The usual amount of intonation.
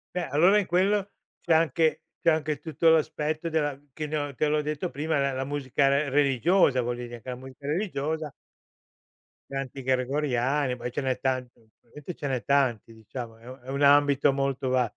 Yes: average, 3.1 semitones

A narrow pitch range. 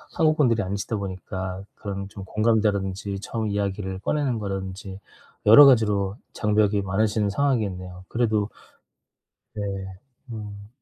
Yes: narrow, 2.2 semitones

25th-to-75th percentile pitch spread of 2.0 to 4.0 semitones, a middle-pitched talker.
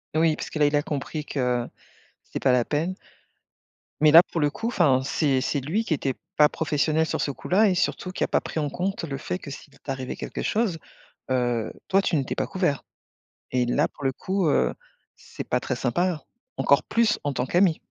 No: average, 4.6 semitones; medium, 150 Hz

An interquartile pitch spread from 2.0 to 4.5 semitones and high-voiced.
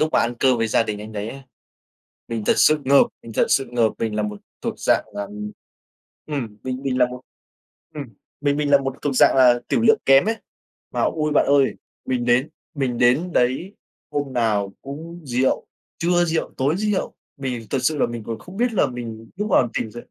No: average, 4.2 semitones; low, 130 Hz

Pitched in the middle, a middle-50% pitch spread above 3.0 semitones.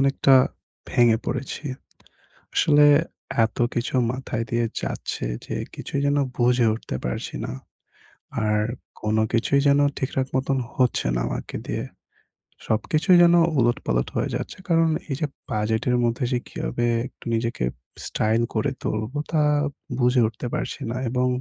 No: low, 120 Hz; average, 3.6 semitones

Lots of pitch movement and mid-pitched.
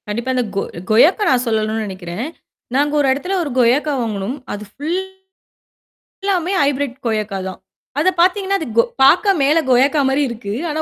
No: wide, 6.1 semitones; very high, 270 Hz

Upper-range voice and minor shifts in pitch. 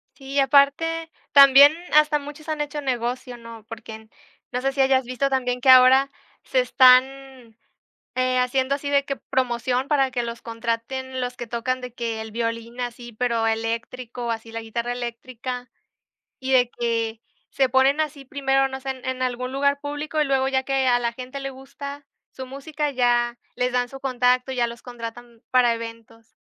Yes: very high, 255 Hz; narrow, 2.3 semitones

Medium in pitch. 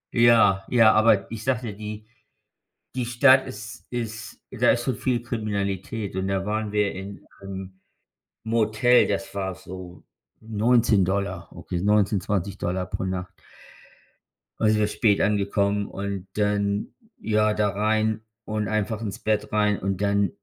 No: low, 105 Hz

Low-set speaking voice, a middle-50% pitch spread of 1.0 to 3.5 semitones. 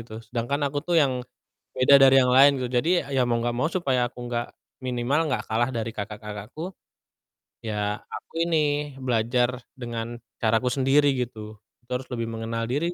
Yes: low, 120 Hz; average, 2.8 semitones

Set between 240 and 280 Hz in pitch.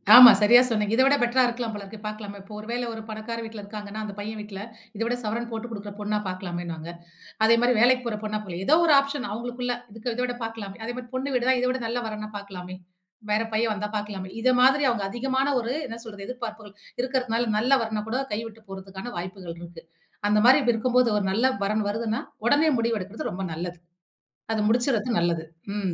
No: high, 220 Hz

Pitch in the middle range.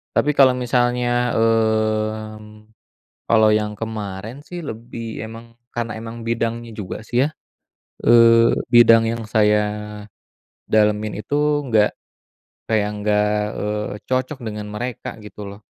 No: low, 110 Hz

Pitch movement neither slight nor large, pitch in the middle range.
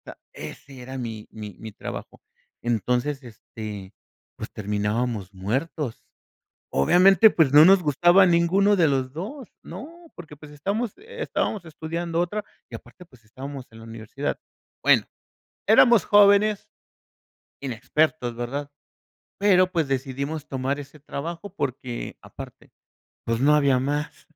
No: wide, 6.4 semitones; medium, 145 Hz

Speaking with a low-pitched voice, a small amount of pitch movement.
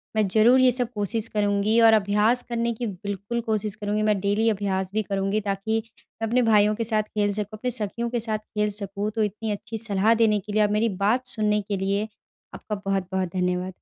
No: high, 210 Hz; narrow, 1.8 semitones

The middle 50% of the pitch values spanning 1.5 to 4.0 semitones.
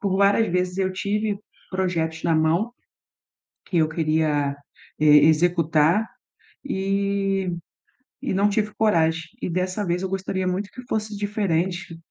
Yes: average, 3.4 semitones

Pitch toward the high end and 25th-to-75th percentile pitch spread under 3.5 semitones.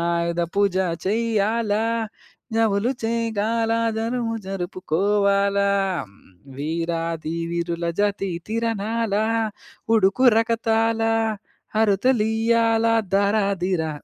Yes: high, 210 Hz; average, 3.0 semitones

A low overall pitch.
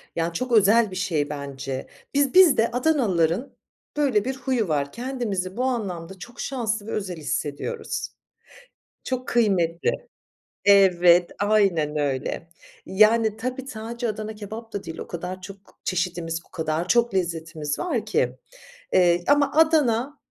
No: high, 205 Hz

